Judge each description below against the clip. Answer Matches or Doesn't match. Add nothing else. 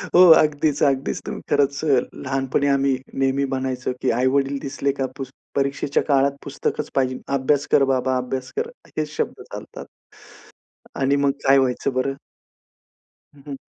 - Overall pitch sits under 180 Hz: Matches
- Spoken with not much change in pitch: Matches